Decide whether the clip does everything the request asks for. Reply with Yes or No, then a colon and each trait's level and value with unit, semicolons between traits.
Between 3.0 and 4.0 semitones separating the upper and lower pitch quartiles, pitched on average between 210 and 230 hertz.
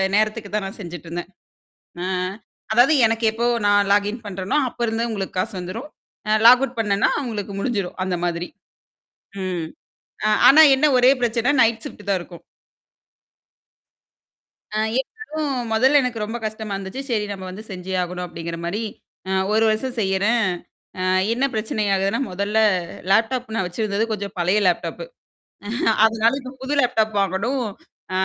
Yes: average, 3.7 semitones; high, 215 Hz